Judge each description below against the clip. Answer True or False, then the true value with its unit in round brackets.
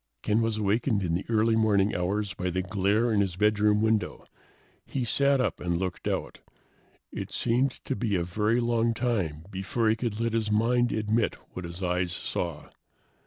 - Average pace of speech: True (180 wpm)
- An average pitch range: True (3.6 semitones)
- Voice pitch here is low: True (105 Hz)